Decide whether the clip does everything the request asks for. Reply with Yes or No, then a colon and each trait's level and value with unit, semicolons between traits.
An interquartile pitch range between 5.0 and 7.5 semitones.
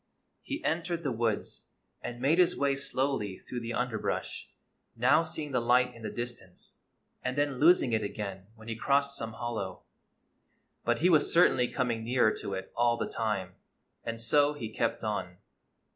No: average, 4.0 semitones